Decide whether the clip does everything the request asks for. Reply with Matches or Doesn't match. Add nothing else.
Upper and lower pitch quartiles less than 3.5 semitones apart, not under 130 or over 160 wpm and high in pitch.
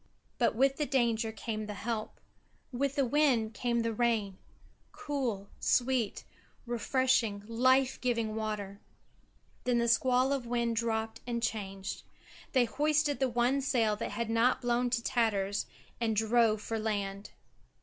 Matches